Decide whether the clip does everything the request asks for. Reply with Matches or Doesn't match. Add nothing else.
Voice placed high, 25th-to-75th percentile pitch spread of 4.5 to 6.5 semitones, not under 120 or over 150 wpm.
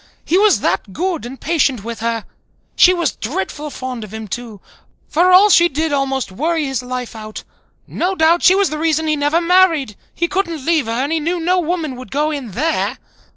Doesn't match